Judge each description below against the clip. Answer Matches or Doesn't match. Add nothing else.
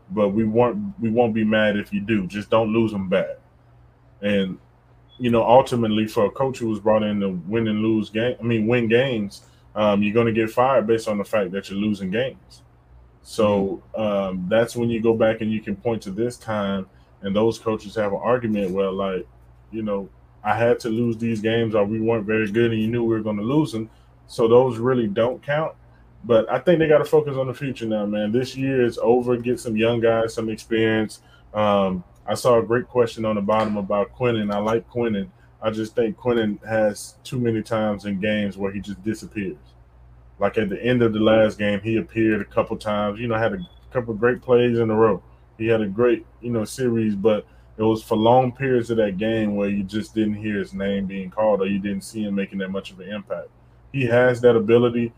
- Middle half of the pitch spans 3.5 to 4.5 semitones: Doesn't match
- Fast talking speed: Matches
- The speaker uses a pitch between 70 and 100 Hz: Doesn't match